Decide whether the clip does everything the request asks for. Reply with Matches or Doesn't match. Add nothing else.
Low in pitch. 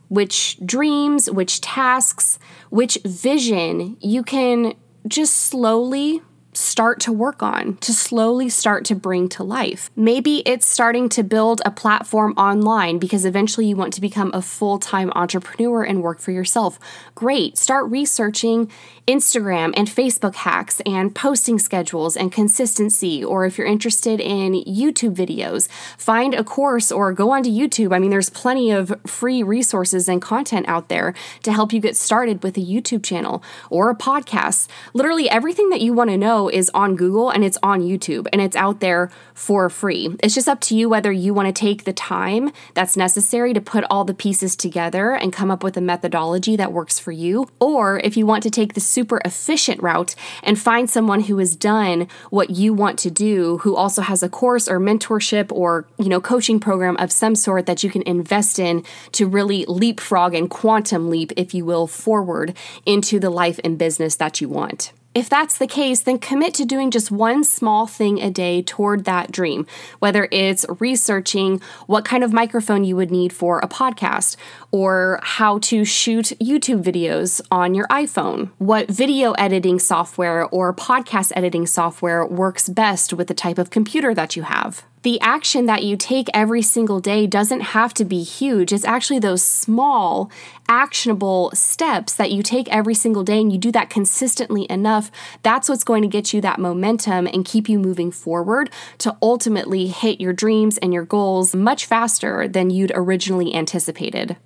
Doesn't match